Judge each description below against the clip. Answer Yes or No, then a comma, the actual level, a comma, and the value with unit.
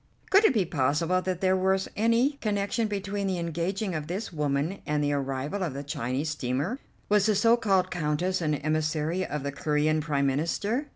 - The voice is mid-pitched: Yes, medium, 170 Hz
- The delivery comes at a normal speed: Yes, average, 185 wpm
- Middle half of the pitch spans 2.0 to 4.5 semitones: No, average, 5.1 semitones